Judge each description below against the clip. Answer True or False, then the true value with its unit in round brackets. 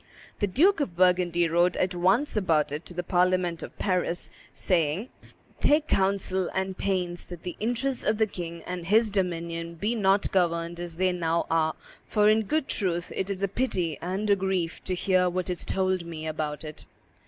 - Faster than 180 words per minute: True (190 wpm)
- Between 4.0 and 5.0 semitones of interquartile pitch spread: False (2.6 semitones)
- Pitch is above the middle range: False (180 Hz)